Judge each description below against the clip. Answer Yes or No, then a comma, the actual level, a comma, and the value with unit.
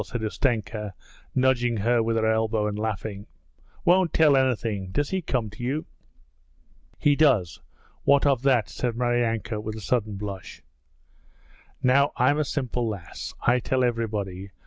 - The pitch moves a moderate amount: Yes, average, 3.7 semitones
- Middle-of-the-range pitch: No, low, 115 Hz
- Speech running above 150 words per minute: No, average, 145 wpm